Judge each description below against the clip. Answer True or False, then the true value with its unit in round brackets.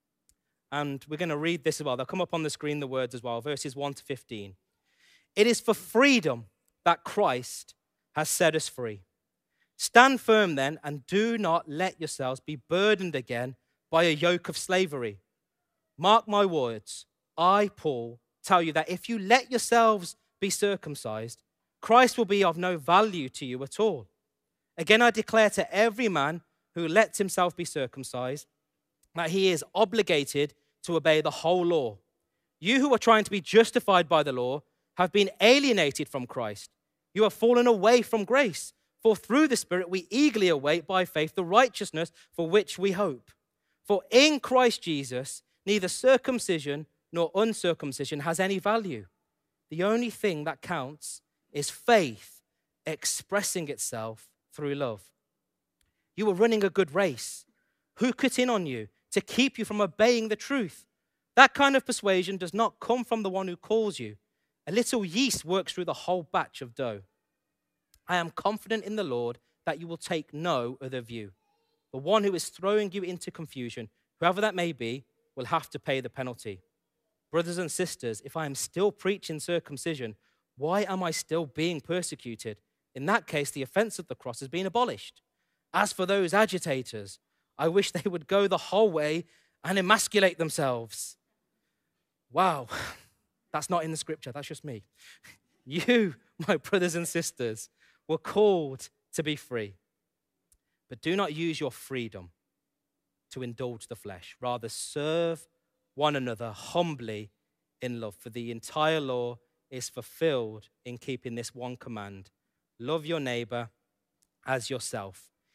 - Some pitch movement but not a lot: False (7.6 semitones)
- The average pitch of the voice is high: False (165 Hz)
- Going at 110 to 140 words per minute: False (165 wpm)